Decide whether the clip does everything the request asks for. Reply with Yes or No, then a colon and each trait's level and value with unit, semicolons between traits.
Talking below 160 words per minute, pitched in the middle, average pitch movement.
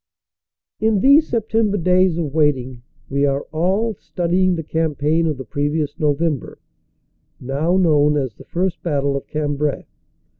Yes: average, 140 wpm; medium, 155 Hz; average, 4.2 semitones